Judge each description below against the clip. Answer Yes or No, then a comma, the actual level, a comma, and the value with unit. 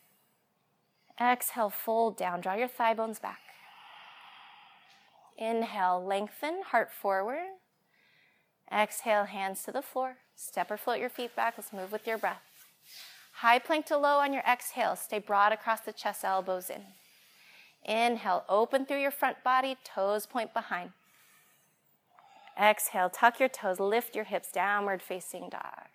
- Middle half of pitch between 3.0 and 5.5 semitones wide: Yes, average, 4.1 semitones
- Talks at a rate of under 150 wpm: Yes, average, 140 wpm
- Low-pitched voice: No, high, 225 Hz